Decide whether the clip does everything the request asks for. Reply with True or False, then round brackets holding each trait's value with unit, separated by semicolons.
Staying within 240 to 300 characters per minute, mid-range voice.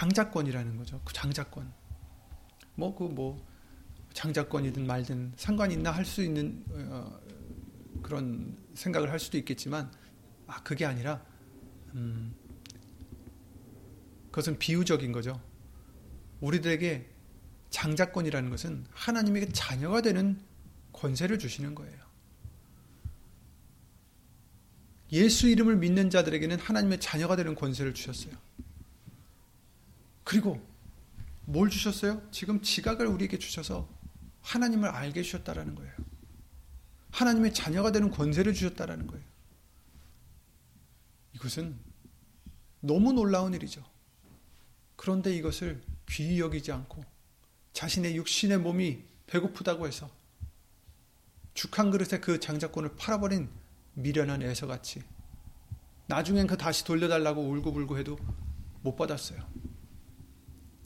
True (250 characters per minute; 150 Hz)